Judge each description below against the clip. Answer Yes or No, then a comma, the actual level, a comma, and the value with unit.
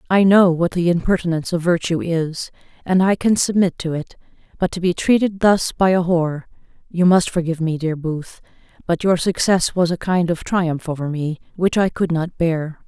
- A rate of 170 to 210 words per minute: Yes, average, 195 wpm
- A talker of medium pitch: Yes, medium, 175 Hz